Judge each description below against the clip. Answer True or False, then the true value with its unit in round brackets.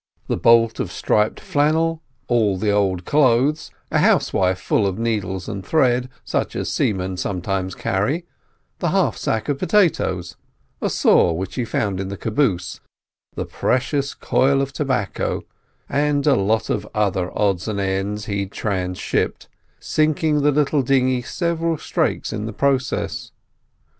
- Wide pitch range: True (6.4 semitones)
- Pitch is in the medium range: False (110 Hz)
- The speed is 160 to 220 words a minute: False (145 wpm)